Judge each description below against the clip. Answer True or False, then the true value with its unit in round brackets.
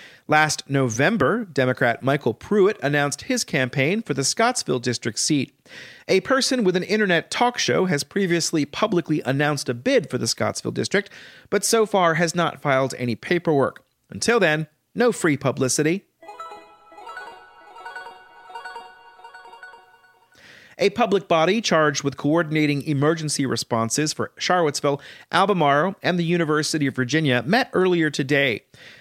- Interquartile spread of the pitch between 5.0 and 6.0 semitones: True (5.3 semitones)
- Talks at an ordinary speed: False (130 wpm)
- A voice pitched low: False (155 Hz)